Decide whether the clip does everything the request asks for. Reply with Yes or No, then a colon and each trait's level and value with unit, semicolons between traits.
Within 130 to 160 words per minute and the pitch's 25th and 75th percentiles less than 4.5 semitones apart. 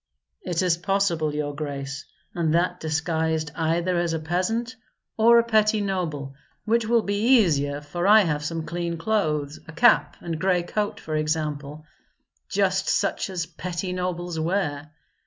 Yes: average, 155 wpm; average, 3.9 semitones